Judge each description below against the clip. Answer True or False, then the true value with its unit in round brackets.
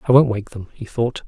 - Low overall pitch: True (120 Hz)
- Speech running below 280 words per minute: False (285 wpm)